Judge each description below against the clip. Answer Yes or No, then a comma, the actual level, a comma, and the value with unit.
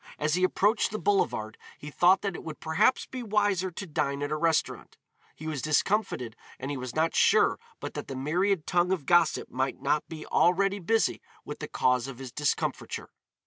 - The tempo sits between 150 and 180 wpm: No, average, 195 wpm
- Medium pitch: Yes, medium, 160 Hz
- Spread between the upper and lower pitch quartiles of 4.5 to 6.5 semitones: Yes, average, 5.1 semitones